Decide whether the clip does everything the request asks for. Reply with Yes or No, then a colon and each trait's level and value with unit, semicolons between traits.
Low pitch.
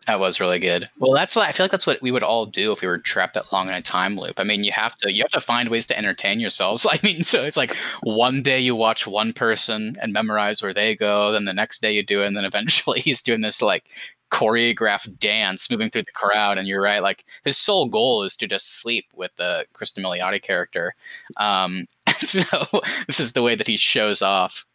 Yes: low, 110 Hz